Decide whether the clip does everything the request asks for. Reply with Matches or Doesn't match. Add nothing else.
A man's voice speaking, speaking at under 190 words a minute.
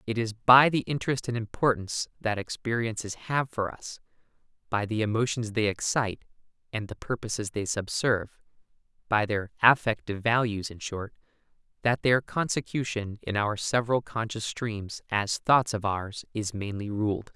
Matches